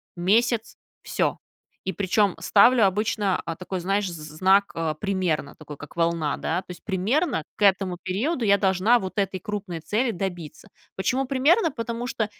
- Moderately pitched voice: No, high, 195 Hz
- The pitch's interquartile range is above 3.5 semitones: Yes, average, 4.2 semitones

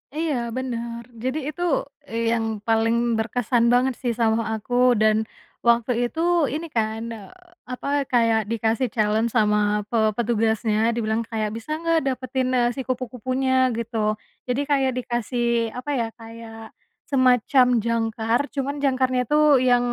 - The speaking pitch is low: No, high, 235 Hz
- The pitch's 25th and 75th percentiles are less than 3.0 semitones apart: Yes, narrow, 2.4 semitones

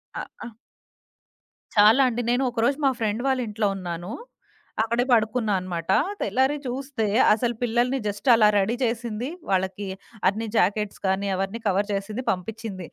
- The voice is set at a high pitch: Yes, high, 220 Hz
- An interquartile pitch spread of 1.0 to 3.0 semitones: No, average, 3.5 semitones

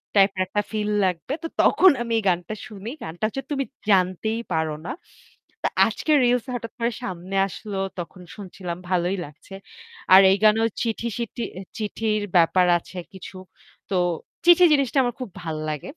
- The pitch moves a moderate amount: Yes, average, 4.2 semitones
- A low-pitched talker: No, high, 205 Hz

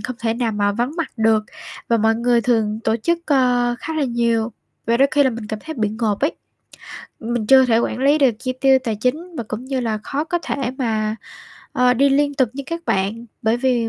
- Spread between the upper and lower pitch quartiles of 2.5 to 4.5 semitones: Yes, average, 3.4 semitones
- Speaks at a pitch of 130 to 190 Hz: No, high, 240 Hz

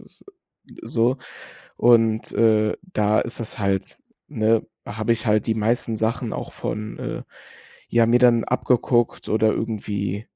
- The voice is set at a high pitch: No, low, 110 Hz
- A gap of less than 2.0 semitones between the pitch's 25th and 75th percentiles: Yes, narrow, 1.6 semitones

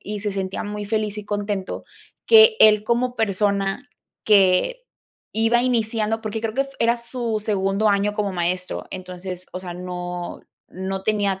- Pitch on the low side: No, high, 205 Hz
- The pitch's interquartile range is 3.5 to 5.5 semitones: No, average, 2.7 semitones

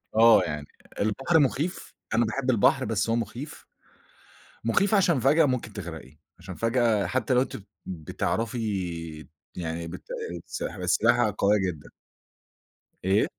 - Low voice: Yes, low, 115 Hz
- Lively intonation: Yes, wide, 5.9 semitones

